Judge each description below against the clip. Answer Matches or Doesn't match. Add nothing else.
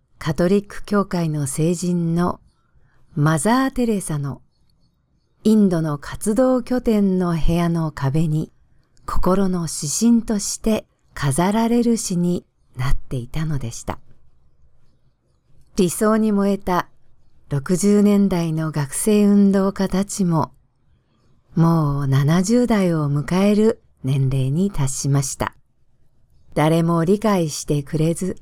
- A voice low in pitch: Doesn't match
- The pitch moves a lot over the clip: Matches